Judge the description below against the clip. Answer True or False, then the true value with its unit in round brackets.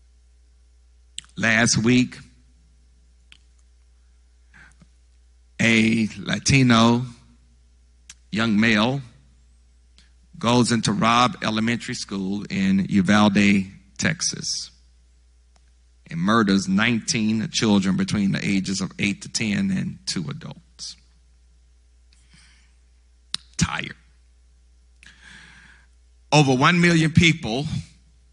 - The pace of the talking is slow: True (70 wpm)